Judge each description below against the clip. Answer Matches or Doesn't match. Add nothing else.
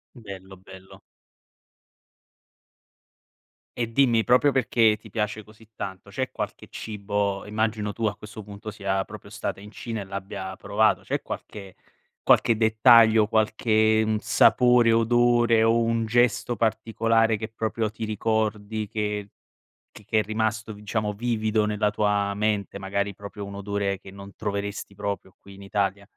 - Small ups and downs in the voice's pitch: Matches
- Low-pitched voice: Matches